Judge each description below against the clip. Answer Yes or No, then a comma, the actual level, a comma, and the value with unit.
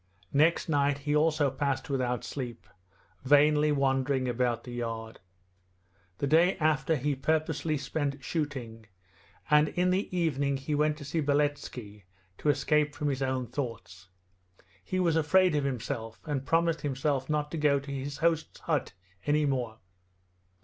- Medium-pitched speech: Yes, medium, 145 Hz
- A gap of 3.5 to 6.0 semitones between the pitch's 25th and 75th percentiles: No, narrow, 2.6 semitones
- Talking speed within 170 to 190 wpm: No, average, 150 wpm